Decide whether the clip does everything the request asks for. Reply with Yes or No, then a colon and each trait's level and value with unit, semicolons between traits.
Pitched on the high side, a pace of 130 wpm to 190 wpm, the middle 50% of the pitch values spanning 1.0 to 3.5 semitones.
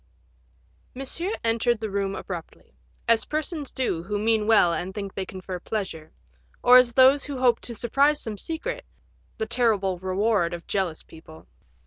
No: high, 220 Hz; average, 155 wpm; average, 4.9 semitones